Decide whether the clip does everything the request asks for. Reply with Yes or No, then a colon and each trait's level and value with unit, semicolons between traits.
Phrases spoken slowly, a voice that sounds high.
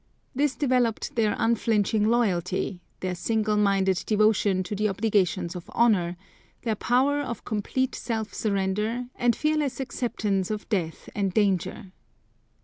Yes: slow, 130 wpm; high, 215 Hz